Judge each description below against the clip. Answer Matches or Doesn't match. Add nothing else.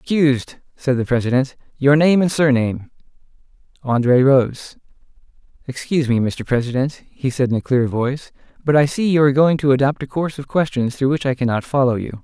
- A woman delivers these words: Doesn't match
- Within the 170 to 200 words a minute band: Matches